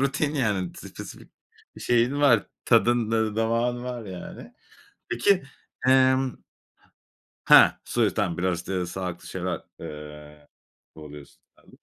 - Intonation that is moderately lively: No, wide, 5.8 semitones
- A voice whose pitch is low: Yes, low, 110 Hz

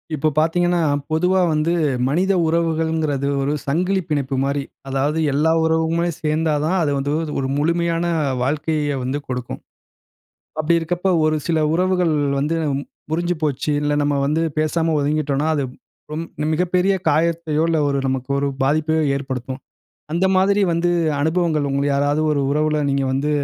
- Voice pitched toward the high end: No, medium, 155 Hz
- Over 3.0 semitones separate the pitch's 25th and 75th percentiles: No, average, 2.7 semitones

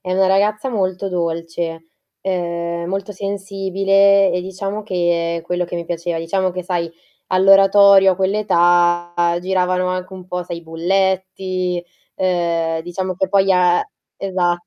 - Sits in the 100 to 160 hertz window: No, medium, 185 Hz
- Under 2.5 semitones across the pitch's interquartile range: Yes, narrow, 1.9 semitones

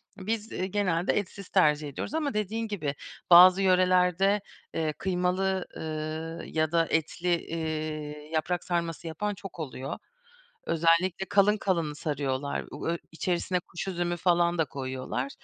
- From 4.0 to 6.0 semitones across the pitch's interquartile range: No, average, 3.3 semitones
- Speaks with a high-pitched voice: No, medium, 170 Hz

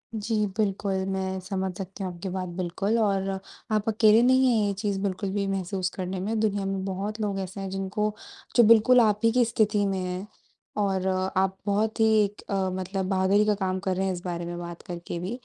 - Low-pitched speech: No, high, 195 Hz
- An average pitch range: No, narrow, 2.1 semitones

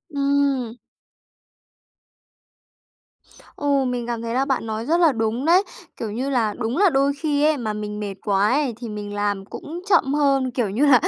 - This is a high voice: Yes, very high, 250 Hz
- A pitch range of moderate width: Yes, average, 4.4 semitones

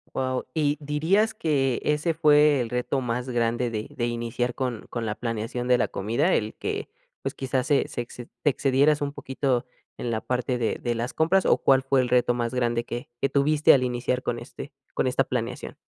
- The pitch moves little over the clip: No, average, 3.1 semitones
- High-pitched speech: No, low, 125 Hz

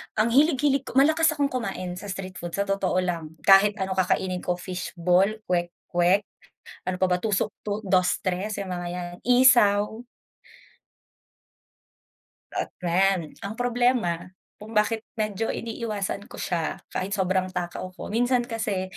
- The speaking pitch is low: No, high, 195 Hz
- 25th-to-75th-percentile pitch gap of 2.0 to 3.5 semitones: No, average, 3.9 semitones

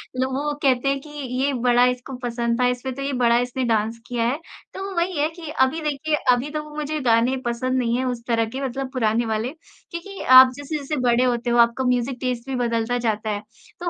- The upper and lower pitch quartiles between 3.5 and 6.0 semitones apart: No, average, 2.8 semitones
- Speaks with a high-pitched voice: Yes, very high, 255 Hz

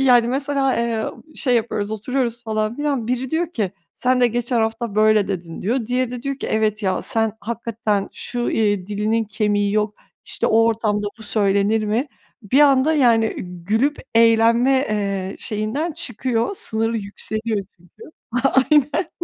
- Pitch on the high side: Yes, high, 225 Hz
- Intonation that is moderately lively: Yes, average, 3.1 semitones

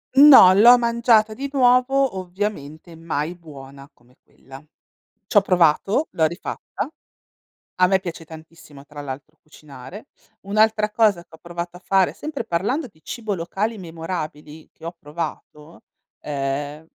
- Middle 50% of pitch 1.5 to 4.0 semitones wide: No, wide, 5.9 semitones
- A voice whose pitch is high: No, medium, 175 Hz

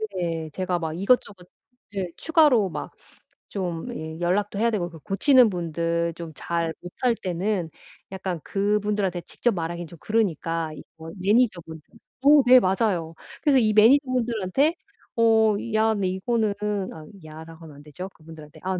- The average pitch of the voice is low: No, medium, 185 Hz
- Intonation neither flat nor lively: Yes, average, 4.8 semitones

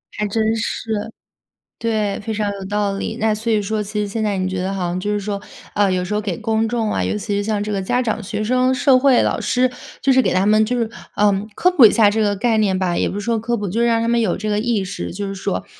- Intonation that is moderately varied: No, narrow, 2.1 semitones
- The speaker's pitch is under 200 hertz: No, high, 210 Hz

